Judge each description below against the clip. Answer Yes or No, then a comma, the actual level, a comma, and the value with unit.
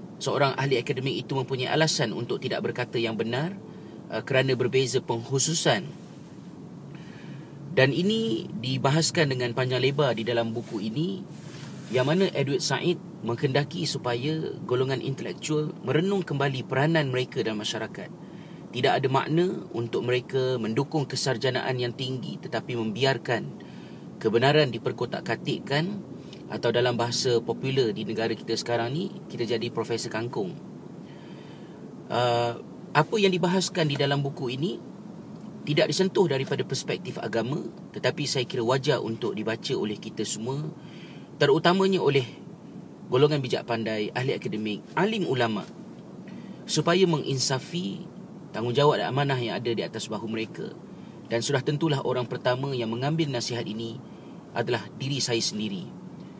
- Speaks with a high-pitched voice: No, low, 135 Hz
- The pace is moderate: Yes, average, 125 wpm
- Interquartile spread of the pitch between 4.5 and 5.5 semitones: Yes, average, 4.8 semitones